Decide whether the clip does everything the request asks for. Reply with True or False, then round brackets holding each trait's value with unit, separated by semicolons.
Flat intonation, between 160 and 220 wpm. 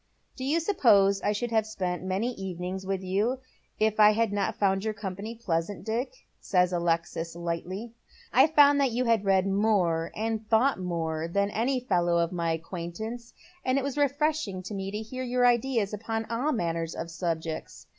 False (4.7 semitones; 190 wpm)